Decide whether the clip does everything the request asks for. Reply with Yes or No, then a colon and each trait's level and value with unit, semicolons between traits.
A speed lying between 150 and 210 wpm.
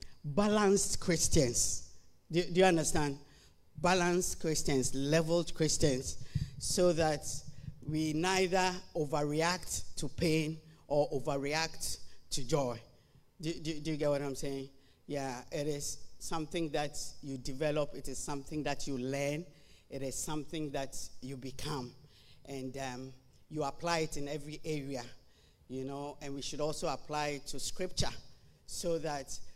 No: average, 140 wpm